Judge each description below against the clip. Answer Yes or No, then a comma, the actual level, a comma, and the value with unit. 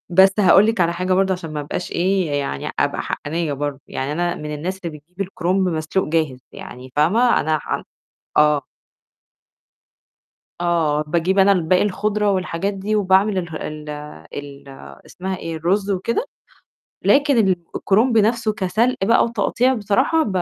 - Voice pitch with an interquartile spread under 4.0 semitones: No, average, 4.3 semitones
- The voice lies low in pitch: No, medium, 185 Hz